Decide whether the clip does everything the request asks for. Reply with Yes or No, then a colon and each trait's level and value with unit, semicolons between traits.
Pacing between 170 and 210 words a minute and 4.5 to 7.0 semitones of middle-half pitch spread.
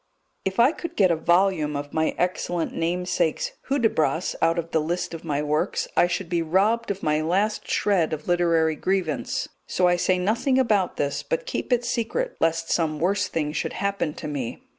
No: average, 190 wpm; average, 3.9 semitones